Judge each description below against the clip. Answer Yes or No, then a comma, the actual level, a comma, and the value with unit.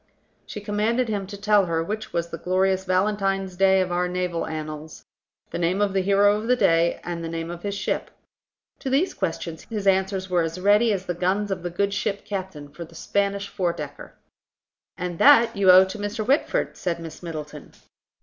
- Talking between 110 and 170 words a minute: No, average, 200 wpm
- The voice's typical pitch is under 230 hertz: Yes, high, 190 Hz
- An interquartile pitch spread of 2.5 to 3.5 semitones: Yes, average, 3.1 semitones